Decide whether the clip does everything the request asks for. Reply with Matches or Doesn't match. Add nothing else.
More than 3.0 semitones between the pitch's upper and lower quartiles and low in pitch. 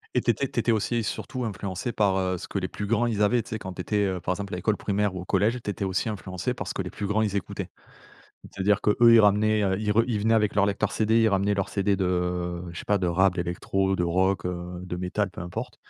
Doesn't match